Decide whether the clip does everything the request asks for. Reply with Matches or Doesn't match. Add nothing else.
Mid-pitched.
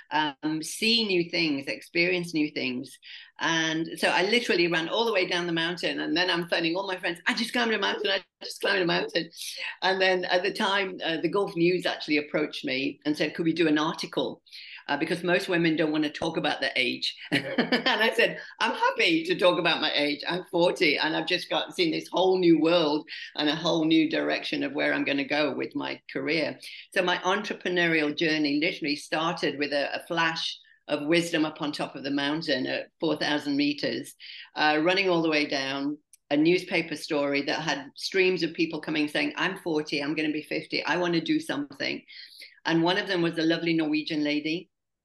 Matches